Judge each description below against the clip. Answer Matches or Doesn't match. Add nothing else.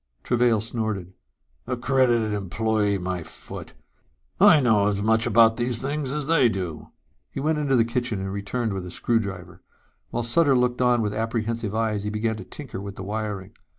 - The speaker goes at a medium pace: Matches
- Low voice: Matches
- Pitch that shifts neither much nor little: Matches